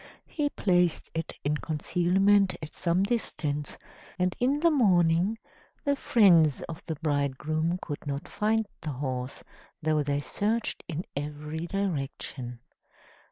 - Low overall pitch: No, medium, 165 Hz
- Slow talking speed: Yes, slow, 125 wpm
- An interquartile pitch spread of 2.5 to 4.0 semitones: No, average, 5.0 semitones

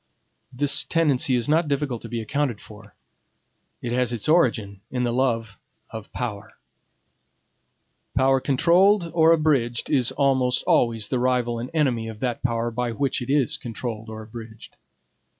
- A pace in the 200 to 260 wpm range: No, average, 150 wpm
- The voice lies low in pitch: Yes, low, 125 Hz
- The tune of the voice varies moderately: Yes, average, 3.5 semitones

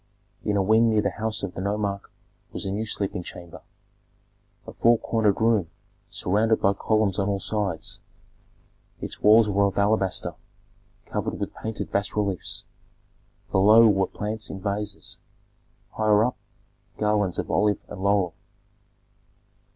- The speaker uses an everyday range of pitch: No, narrow, 1.8 semitones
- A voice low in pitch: Yes, low, 105 Hz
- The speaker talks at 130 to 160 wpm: Yes, average, 140 wpm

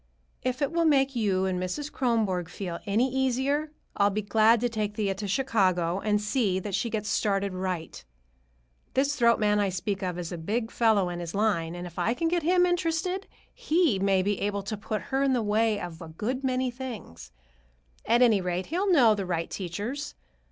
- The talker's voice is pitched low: No, high, 210 Hz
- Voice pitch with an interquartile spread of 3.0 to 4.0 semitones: No, wide, 5.5 semitones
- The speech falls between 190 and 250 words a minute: Yes, average, 200 wpm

